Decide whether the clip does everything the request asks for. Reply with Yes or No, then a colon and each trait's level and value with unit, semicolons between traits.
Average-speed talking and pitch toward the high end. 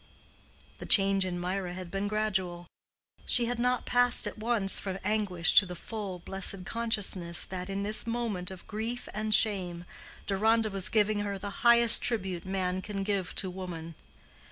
Yes: average, 165 wpm; high, 195 Hz